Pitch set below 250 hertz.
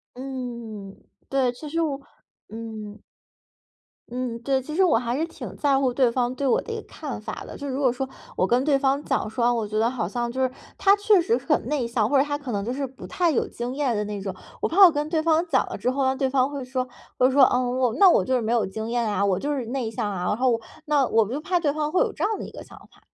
No: very high, 255 Hz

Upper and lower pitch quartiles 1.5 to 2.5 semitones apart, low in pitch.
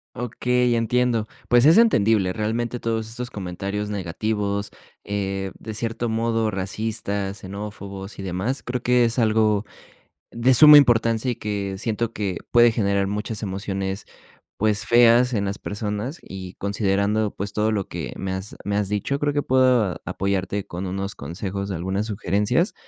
No: average, 2.9 semitones; low, 105 Hz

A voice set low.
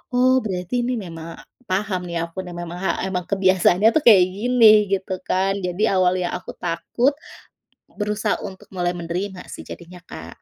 No: high, 190 Hz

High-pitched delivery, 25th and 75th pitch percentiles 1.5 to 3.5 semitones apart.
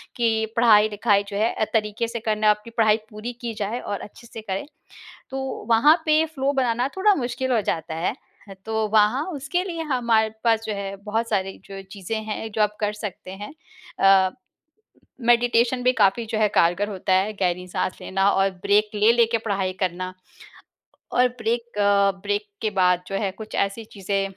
Yes: high, 215 Hz; average, 2.9 semitones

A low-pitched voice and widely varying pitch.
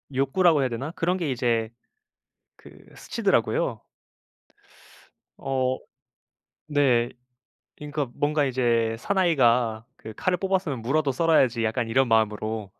No: low, 130 Hz; average, 4.7 semitones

